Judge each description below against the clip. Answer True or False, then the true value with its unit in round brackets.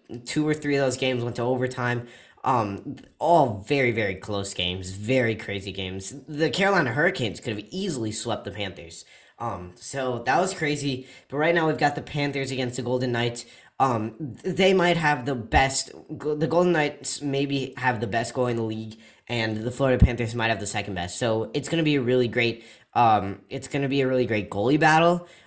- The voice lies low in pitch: True (125 Hz)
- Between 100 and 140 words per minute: False (205 wpm)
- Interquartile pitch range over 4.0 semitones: True (4.5 semitones)